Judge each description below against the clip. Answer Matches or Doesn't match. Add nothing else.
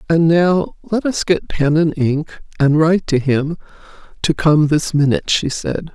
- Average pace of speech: Matches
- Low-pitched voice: Doesn't match